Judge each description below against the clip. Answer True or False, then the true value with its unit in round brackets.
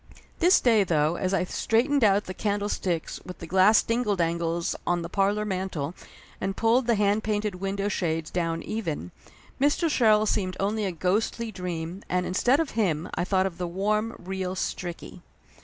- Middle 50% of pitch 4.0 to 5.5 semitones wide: False (3.4 semitones)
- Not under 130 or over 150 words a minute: False (180 wpm)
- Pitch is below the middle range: False (195 Hz)